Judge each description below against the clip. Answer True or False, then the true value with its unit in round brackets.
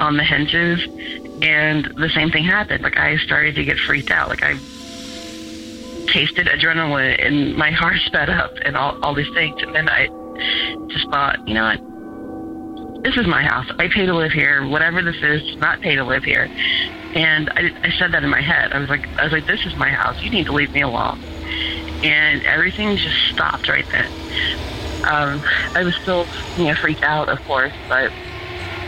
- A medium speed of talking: True (195 wpm)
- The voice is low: False (155 Hz)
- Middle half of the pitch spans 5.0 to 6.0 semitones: False (4.2 semitones)